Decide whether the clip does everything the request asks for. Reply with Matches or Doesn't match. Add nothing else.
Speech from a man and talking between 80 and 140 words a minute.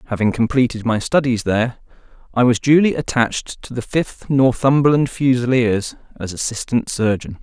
Matches